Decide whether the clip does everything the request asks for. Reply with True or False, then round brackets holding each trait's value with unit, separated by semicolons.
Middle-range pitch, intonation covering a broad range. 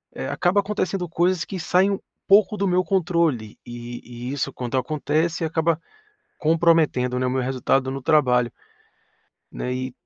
True (155 Hz; 5.8 semitones)